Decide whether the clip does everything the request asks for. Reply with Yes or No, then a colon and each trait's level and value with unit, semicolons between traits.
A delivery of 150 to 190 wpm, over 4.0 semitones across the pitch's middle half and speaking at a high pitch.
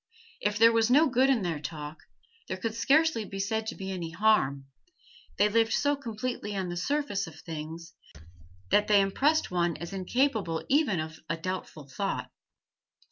Yes: average, 170 wpm; wide, 5.4 semitones; high, 200 Hz